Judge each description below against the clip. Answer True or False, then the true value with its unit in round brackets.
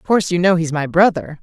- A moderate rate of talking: False (295 wpm)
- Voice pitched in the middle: True (170 Hz)